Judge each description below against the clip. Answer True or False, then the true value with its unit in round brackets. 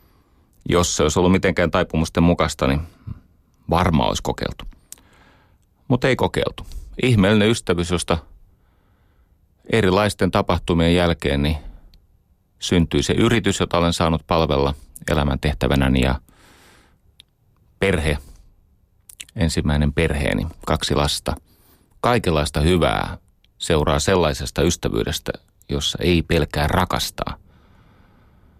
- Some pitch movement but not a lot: True (3.8 semitones)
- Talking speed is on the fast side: False (95 wpm)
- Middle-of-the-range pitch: False (85 Hz)